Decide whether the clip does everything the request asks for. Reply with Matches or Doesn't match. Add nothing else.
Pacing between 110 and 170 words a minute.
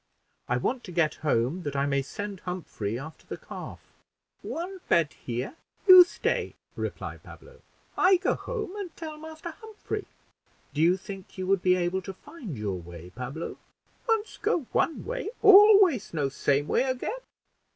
Matches